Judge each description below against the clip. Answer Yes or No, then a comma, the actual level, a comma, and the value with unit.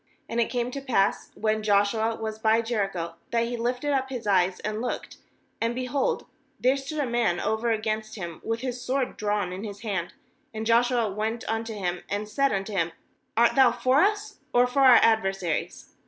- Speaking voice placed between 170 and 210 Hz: No, high, 225 Hz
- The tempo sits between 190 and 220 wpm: Yes, average, 195 wpm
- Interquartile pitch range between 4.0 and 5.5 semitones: No, average, 3.3 semitones